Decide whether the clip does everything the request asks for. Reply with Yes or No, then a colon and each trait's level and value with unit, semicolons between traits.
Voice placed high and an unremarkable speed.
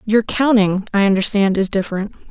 Yes: high, 205 Hz; average, 155 wpm